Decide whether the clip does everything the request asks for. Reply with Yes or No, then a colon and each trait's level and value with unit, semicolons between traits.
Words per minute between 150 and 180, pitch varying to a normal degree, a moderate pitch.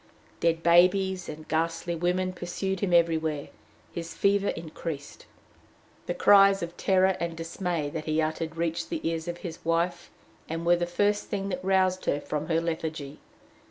No: average, 160 wpm; narrow, 2.2 semitones; medium, 170 Hz